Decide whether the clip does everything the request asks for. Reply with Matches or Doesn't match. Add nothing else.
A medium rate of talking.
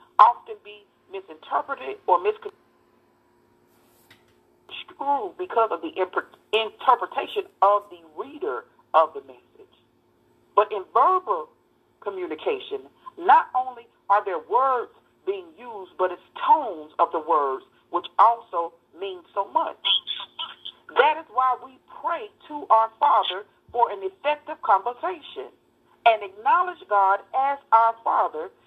Doesn't match